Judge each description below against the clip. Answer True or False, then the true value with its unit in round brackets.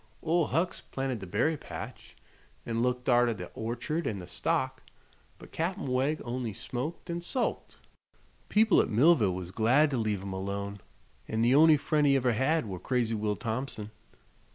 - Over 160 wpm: True (170 wpm)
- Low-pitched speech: True (125 Hz)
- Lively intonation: True (5.8 semitones)